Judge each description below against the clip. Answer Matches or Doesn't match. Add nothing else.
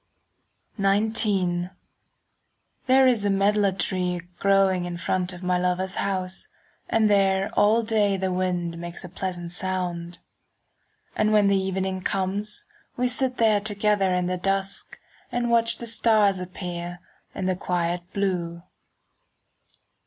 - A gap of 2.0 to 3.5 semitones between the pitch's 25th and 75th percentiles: Matches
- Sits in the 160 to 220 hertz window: Matches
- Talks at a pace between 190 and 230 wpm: Doesn't match